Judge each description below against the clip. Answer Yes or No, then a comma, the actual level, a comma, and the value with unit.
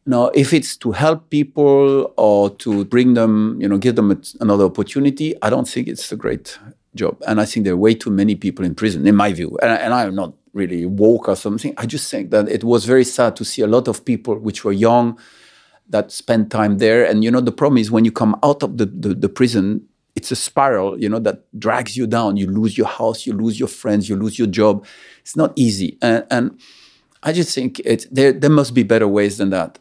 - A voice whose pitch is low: Yes, low, 110 Hz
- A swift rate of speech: Yes, fast, 240 wpm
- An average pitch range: Yes, average, 3.6 semitones